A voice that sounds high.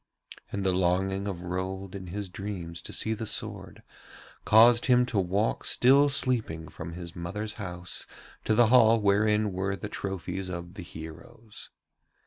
No: low, 100 Hz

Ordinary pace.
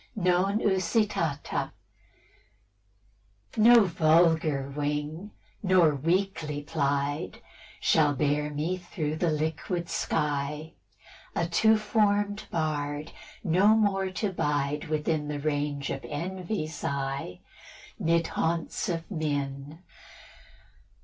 No: slow, 95 wpm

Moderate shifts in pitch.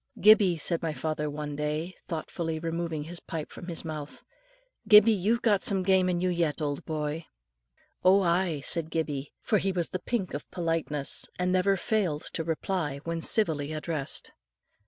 Yes: average, 3.4 semitones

